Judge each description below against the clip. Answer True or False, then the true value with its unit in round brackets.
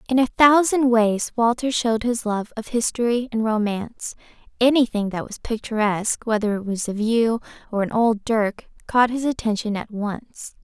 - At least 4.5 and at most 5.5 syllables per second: True (4.8 syllables/s)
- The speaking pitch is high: True (225 Hz)